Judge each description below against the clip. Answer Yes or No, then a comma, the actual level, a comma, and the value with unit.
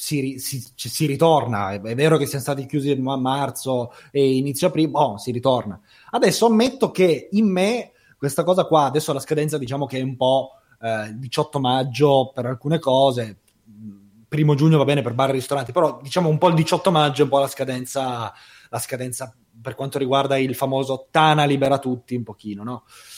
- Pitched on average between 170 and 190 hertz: No, low, 135 Hz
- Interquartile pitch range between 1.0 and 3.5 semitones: Yes, average, 3.1 semitones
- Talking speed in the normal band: No, fast, 190 wpm